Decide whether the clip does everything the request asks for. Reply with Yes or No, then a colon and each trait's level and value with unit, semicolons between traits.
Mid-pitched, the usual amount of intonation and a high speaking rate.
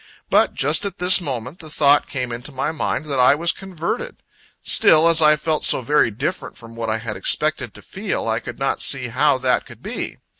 Yes: medium, 145 Hz; average, 4.3 semitones; fast, 215 wpm